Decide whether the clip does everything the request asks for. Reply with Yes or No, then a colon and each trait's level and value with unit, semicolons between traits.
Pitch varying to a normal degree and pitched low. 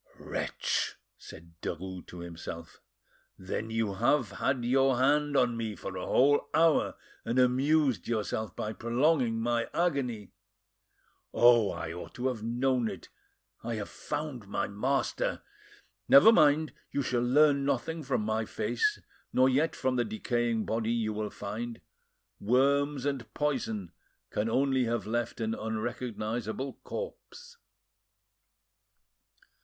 Yes: average, 4.1 semitones; low, 120 Hz